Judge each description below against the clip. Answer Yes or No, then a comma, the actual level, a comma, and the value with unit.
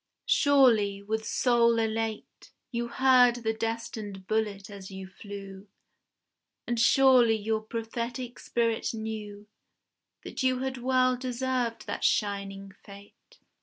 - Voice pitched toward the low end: No, high, 225 Hz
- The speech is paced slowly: Yes, slow, 115 wpm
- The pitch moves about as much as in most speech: Yes, average, 3.1 semitones